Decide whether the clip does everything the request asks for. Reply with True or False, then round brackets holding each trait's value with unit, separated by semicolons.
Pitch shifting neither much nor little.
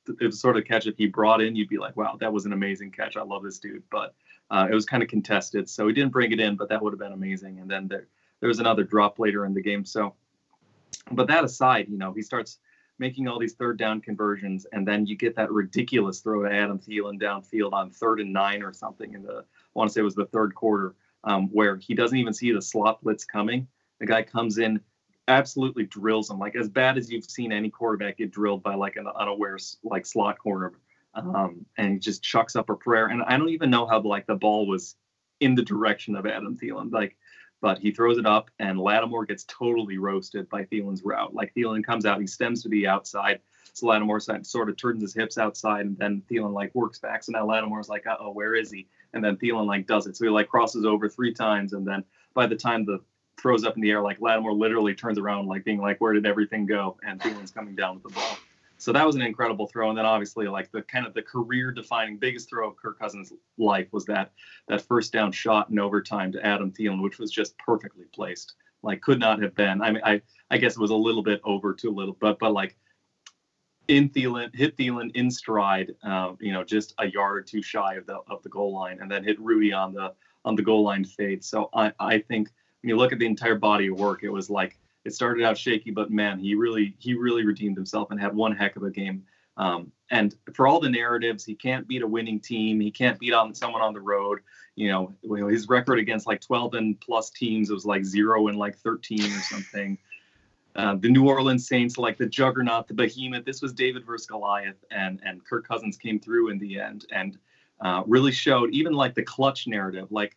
False (2.2 semitones)